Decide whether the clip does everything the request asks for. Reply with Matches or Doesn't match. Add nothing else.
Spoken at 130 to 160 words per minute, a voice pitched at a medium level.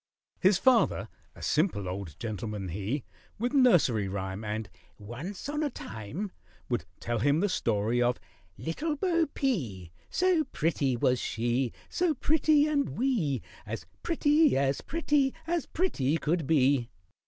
Matches